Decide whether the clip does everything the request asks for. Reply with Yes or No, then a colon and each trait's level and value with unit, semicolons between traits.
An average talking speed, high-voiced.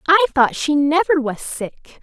Yes: average, 180 wpm; very high, 305 Hz